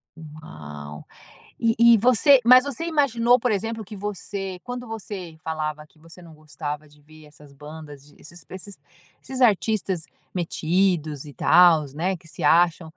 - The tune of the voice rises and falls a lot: Yes, wide, 6.3 semitones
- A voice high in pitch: No, medium, 175 Hz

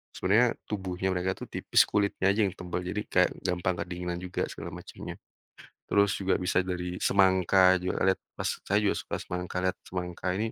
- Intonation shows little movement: Yes, narrow, 1.5 semitones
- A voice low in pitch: Yes, very low, 95 Hz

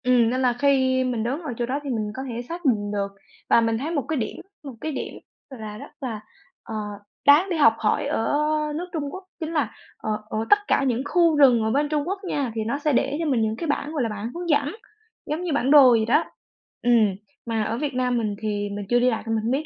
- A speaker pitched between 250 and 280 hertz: Yes, very high, 255 Hz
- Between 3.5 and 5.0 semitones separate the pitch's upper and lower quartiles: Yes, average, 4.6 semitones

